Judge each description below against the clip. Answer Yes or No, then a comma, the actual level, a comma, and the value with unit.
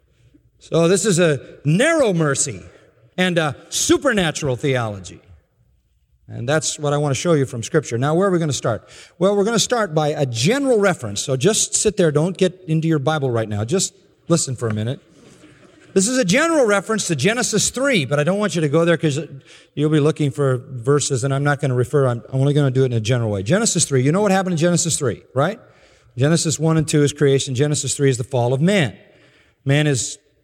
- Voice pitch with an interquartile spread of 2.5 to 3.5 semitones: No, average, 5.1 semitones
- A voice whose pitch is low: No, medium, 150 Hz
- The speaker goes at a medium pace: No, fast, 225 wpm